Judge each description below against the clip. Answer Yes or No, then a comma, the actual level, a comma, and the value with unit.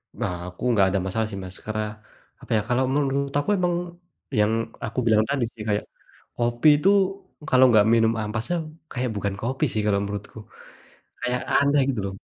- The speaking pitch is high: No, low, 115 Hz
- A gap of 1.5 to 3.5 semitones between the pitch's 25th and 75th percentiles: No, average, 4.2 semitones